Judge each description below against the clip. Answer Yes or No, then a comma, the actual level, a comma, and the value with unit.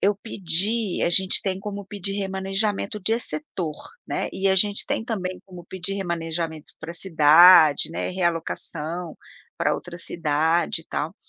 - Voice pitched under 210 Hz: Yes, medium, 185 Hz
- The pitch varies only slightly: No, average, 3.0 semitones